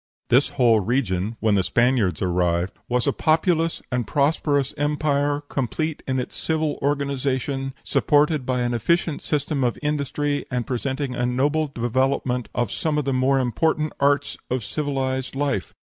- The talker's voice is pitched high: No, low, 135 Hz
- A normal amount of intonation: Yes, average, 3.0 semitones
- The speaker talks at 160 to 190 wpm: No, average, 150 wpm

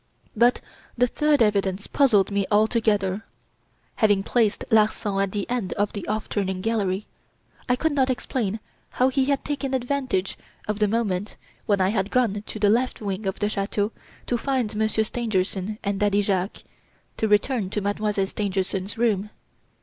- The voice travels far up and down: No, average, 3.1 semitones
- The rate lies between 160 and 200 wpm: Yes, average, 165 wpm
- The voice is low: No, high, 210 Hz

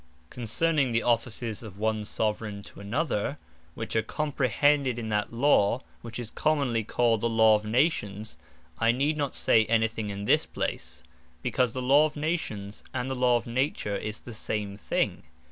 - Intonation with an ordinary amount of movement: Yes, average, 3.6 semitones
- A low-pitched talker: Yes, low, 115 Hz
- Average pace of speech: Yes, average, 175 wpm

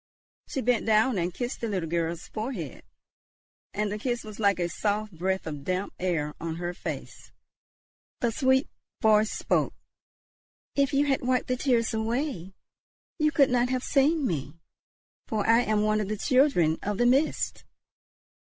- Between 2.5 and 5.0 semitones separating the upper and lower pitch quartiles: No, wide, 5.6 semitones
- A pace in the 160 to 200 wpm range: Yes, average, 165 wpm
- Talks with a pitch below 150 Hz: No, high, 215 Hz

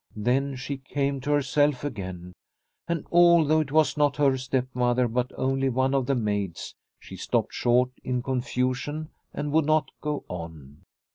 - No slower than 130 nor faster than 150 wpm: No, average, 160 wpm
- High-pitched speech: No, low, 135 Hz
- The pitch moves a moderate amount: Yes, average, 3.0 semitones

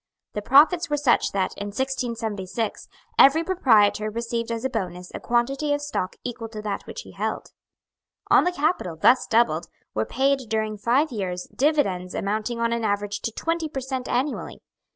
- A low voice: No, high, 235 Hz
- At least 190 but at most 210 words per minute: No, average, 175 wpm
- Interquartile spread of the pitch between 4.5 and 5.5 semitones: Yes, average, 4.8 semitones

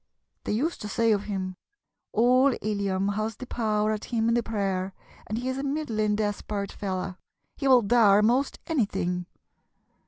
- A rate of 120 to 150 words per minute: No, average, 165 wpm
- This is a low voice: No, high, 215 Hz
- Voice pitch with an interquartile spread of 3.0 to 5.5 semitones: Yes, average, 3.3 semitones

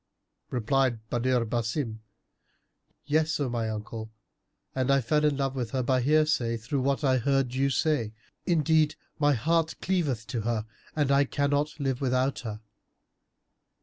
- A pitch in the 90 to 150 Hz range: Yes, low, 135 Hz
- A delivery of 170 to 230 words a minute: No, average, 150 wpm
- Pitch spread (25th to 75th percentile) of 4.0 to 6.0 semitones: No, average, 3.6 semitones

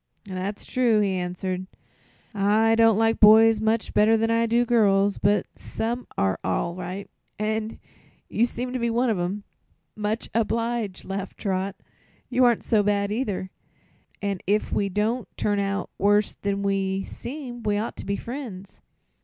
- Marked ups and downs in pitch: No, narrow, 2.5 semitones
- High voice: Yes, high, 210 Hz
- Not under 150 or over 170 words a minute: Yes, average, 160 wpm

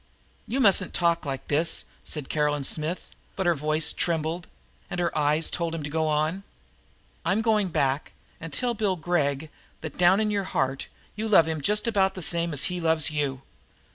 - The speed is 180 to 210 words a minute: Yes, average, 185 wpm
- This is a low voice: No, medium, 165 Hz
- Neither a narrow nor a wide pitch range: Yes, average, 3.8 semitones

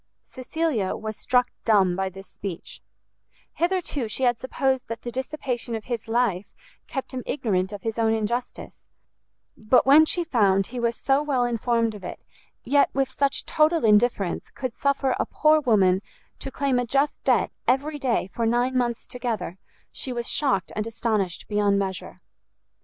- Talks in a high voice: Yes, high, 240 Hz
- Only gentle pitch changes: No, average, 4.1 semitones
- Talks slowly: No, average, 165 wpm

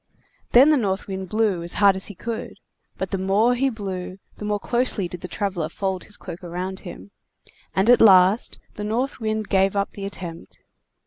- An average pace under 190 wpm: No, average, 195 wpm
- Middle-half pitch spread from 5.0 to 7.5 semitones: No, average, 2.8 semitones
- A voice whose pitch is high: Yes, high, 195 Hz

